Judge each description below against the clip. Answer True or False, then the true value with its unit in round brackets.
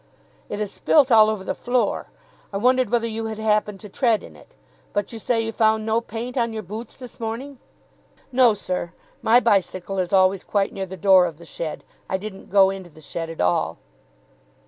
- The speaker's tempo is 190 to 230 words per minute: True (205 wpm)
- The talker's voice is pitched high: True (215 Hz)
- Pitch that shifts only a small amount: False (3.3 semitones)